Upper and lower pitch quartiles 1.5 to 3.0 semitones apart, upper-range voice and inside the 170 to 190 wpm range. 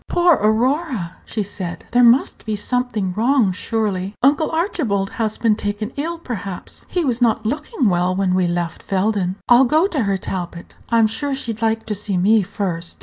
No: average, 4.8 semitones; high, 220 Hz; average, 180 wpm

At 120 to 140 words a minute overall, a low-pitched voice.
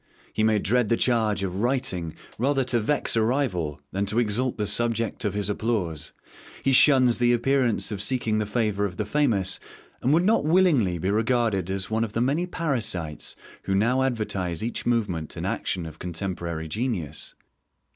No: average, 175 wpm; low, 110 Hz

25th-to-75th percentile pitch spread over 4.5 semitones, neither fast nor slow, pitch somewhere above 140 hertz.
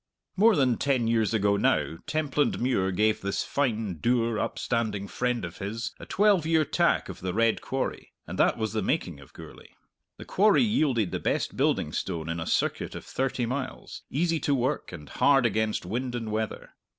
No: average, 5.2 semitones; average, 185 wpm; low, 115 Hz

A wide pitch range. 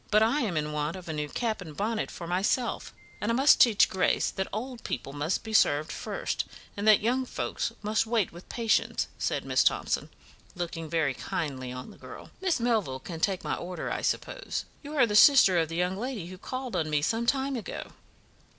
Yes: wide, 6.2 semitones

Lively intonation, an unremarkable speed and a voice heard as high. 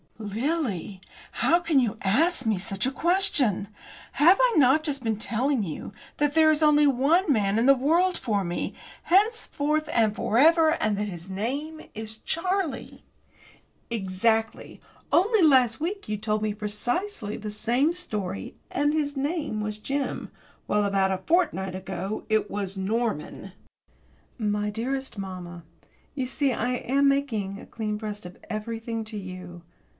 Yes: wide, 6.3 semitones; average, 150 wpm; high, 230 Hz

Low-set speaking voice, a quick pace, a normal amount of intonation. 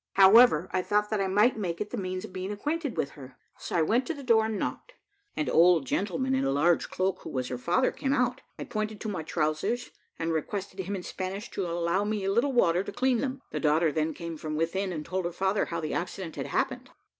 No: high, 190 Hz; fast, 245 wpm; average, 4.7 semitones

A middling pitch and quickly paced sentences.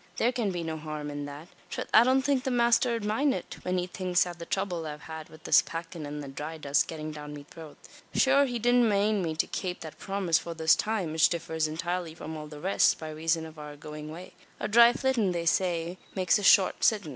Yes: medium, 170 Hz; fast, 240 wpm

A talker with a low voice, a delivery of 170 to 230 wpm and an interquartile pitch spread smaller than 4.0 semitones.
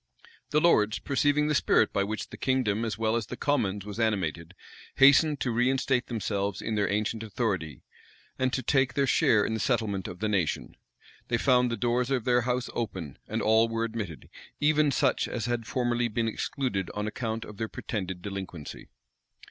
Yes: low, 115 Hz; average, 185 wpm; average, 3.6 semitones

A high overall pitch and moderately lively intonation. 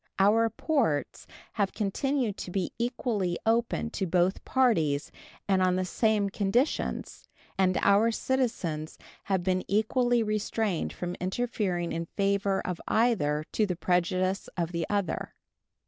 Yes: high, 195 Hz; average, 4.0 semitones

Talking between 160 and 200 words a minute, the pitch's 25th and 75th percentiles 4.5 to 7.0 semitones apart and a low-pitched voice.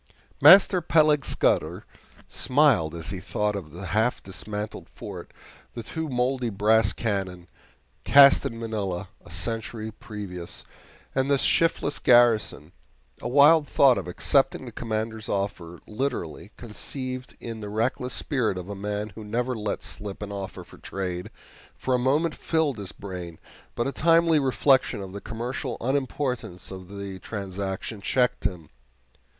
No: average, 145 wpm; average, 5.0 semitones; low, 110 Hz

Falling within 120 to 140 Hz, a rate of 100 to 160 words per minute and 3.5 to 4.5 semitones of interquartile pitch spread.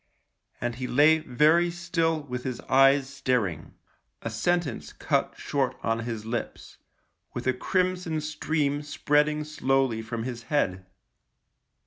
Yes: low, 135 Hz; slow, 135 wpm; average, 4.1 semitones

